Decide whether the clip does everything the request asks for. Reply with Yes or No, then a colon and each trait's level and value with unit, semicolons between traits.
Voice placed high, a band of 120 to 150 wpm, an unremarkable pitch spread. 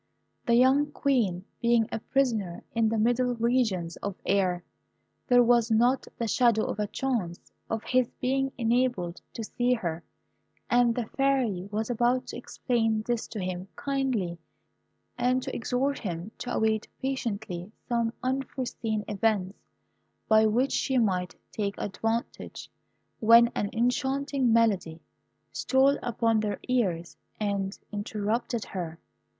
Yes: high, 230 Hz; slow, 135 wpm; average, 3.5 semitones